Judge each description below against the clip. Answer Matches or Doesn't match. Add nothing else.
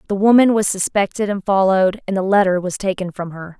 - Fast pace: Matches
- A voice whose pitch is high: Matches